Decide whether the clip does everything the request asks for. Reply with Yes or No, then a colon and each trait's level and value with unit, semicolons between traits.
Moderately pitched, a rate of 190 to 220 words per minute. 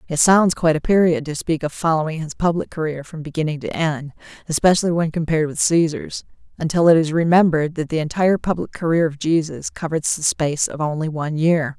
Yes: medium, 160 Hz; average, 200 wpm